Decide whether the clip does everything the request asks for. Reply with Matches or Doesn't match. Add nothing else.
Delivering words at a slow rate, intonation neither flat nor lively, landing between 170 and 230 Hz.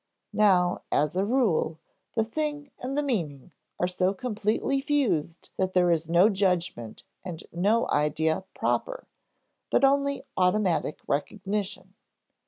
Doesn't match